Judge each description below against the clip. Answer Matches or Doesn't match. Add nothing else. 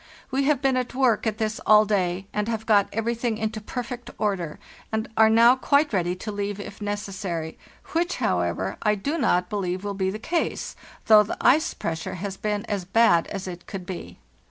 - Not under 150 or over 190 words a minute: Doesn't match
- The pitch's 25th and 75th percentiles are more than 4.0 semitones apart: Doesn't match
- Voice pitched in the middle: Doesn't match